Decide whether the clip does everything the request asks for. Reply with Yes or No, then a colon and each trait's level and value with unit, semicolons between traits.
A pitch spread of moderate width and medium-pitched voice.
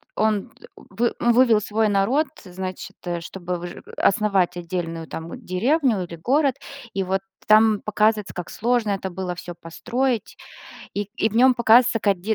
No: average, 4.2 semitones; high, 205 Hz